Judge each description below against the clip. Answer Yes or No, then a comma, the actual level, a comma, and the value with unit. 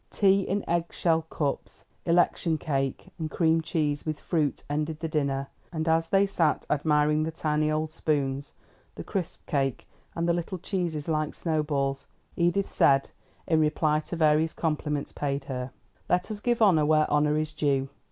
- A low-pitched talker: No, medium, 155 Hz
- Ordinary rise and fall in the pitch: No, narrow, 2.2 semitones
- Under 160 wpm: No, average, 170 wpm